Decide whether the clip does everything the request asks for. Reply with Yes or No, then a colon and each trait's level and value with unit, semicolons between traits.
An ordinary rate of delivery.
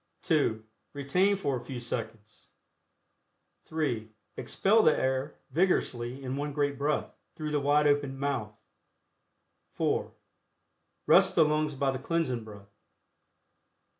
No: slow, 120 wpm